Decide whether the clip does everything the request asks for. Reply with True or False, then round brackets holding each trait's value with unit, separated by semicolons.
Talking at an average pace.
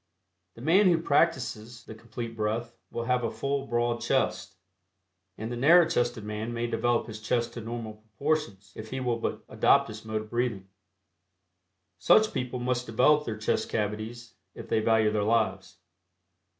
True (165 wpm)